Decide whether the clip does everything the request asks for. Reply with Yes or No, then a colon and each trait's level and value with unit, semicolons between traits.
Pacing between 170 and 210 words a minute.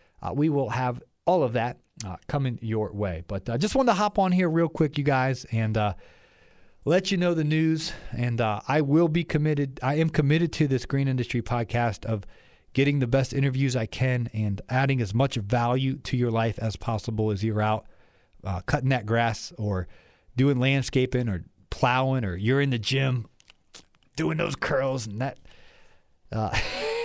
Yes: average, 190 wpm